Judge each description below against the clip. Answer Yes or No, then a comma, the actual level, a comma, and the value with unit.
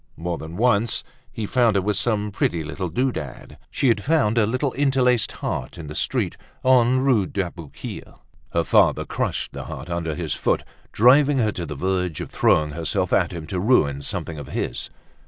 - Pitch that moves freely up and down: Yes, wide, 6.7 semitones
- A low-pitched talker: Yes, low, 100 Hz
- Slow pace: No, average, 185 wpm